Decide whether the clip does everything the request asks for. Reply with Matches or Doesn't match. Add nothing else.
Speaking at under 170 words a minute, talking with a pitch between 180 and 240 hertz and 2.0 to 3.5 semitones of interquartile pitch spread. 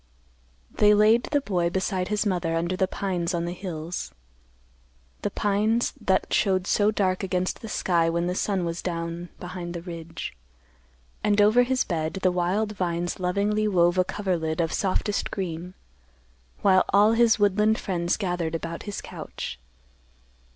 Matches